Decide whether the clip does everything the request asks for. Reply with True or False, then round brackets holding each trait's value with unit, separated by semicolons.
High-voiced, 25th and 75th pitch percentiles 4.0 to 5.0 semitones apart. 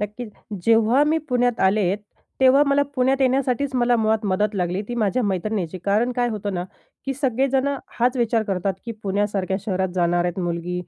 True (220 Hz; 4.7 semitones)